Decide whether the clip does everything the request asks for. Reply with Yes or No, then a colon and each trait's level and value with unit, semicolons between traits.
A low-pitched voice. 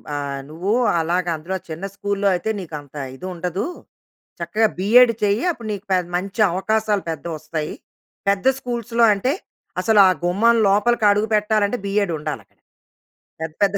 No: high, 200 Hz